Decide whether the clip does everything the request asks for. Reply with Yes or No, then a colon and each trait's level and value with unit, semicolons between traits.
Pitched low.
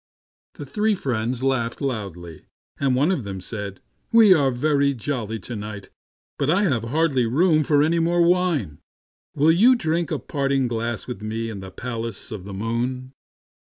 Yes: low, 130 Hz